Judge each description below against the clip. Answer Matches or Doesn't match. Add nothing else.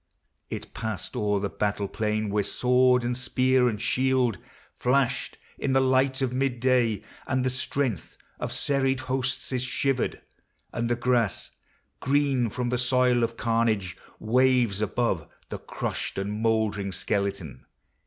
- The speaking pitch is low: Matches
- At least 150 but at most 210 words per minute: Doesn't match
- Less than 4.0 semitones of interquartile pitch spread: Matches